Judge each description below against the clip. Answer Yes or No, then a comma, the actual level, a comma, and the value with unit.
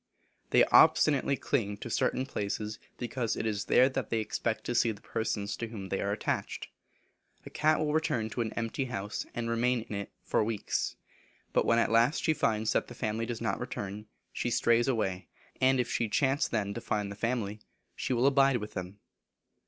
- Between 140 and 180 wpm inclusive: No, average, 195 wpm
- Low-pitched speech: Yes, low, 115 Hz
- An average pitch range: Yes, average, 3.0 semitones